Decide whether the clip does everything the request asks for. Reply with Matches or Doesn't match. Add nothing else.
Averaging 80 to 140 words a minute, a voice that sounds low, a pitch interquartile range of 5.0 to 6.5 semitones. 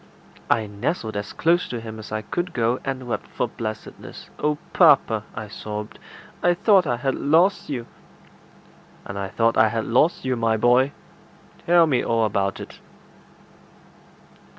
Doesn't match